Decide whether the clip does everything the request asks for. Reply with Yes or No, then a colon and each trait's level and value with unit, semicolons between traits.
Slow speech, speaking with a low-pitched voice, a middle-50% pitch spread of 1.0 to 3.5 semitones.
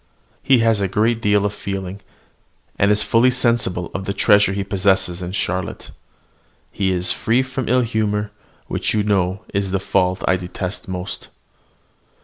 No: average, 160 wpm; low, 100 Hz; average, 2.7 semitones